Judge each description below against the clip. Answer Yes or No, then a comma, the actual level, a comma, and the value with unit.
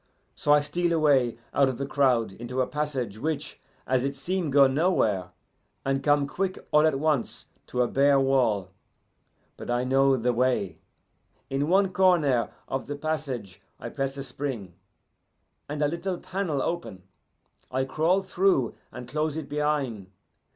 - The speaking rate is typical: Yes, average, 160 wpm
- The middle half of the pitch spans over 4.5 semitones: No, average, 3.5 semitones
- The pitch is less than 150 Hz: Yes, medium, 140 Hz